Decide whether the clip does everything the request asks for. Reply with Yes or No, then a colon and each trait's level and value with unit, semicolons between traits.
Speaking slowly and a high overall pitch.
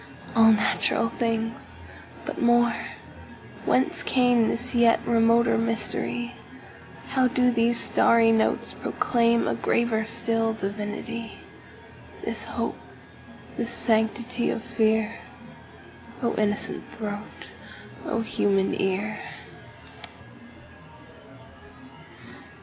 Yes: slow, 70 wpm; high, 230 Hz